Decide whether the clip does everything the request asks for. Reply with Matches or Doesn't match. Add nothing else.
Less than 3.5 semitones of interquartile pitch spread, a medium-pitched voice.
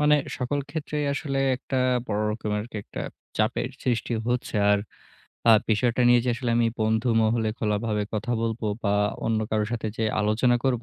Doesn't match